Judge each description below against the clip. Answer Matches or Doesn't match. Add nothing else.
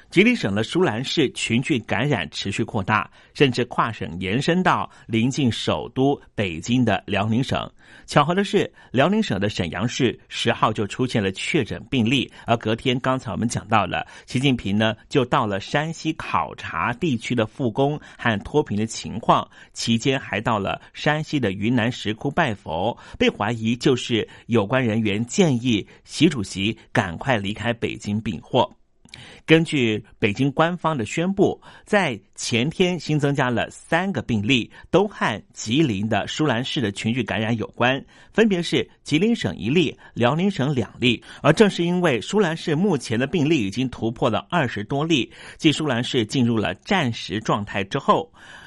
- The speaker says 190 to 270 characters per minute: Matches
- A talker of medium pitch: Doesn't match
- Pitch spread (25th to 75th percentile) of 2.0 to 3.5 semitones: Doesn't match